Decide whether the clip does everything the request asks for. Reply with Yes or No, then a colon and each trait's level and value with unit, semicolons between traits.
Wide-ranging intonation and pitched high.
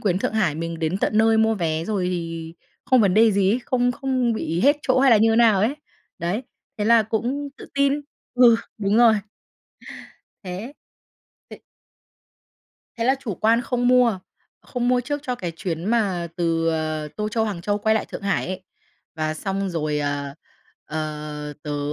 Yes: wide, 5.9 semitones; high, 205 Hz